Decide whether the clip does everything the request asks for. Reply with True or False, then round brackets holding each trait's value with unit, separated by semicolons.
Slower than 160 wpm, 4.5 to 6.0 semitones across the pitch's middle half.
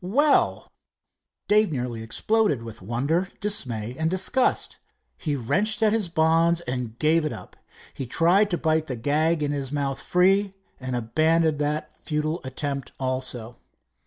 True (145 wpm; 5.3 semitones)